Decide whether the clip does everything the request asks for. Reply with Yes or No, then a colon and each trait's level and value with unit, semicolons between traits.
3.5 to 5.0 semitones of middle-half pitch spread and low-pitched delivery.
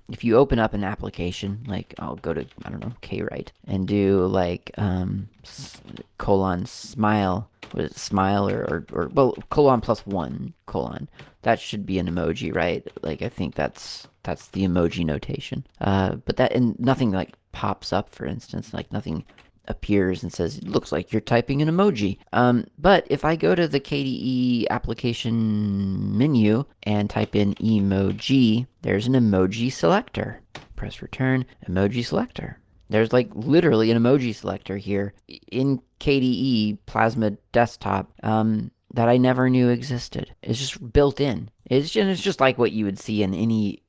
Yes: average, 4.2 semitones; low, 110 Hz